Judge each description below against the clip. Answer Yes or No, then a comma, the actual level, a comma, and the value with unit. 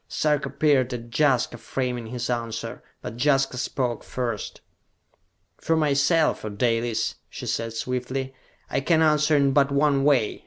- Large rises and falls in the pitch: No, average, 3.5 semitones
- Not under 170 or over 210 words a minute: No, average, 145 wpm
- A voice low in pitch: Yes, low, 130 Hz